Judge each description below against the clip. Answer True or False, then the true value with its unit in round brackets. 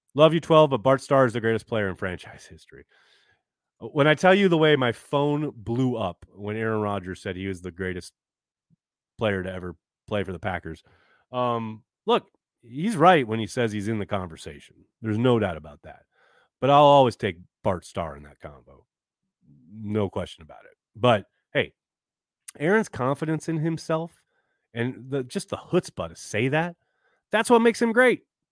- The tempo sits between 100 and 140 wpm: False (180 wpm)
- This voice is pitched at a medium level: False (115 Hz)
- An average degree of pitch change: False (7.7 semitones)